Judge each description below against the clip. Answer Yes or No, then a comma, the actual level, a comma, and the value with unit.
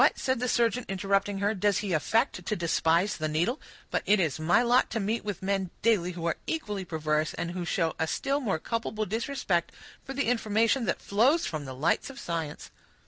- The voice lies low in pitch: No, high, 200 Hz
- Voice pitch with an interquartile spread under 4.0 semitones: No, wide, 5.4 semitones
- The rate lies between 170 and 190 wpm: No, average, 200 wpm